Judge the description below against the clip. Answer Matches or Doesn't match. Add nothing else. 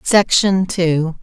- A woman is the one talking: Matches